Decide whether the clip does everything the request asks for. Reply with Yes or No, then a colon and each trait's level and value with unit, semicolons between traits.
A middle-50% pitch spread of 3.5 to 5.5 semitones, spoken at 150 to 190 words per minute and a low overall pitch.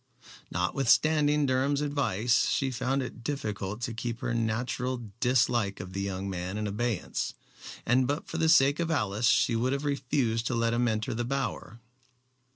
Yes: average, 3.9 semitones; average, 165 wpm; low, 120 Hz